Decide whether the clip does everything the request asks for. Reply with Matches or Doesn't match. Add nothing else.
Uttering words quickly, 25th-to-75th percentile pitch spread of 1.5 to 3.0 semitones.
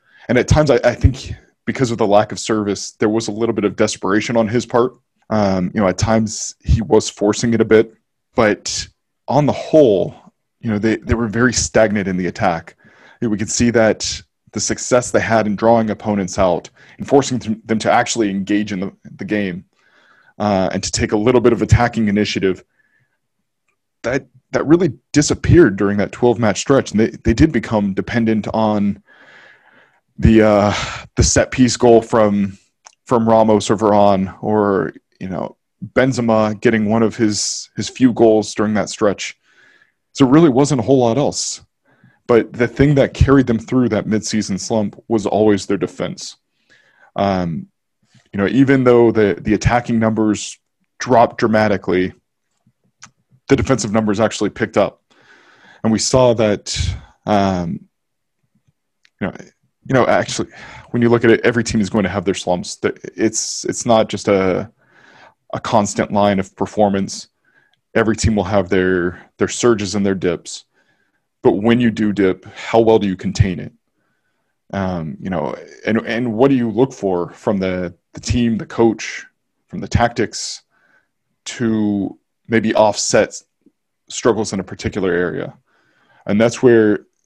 Doesn't match